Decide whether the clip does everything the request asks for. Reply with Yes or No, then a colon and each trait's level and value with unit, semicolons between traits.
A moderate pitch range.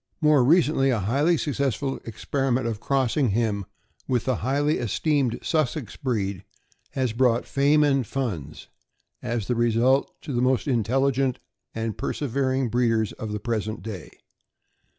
Yes: average, 3.4 semitones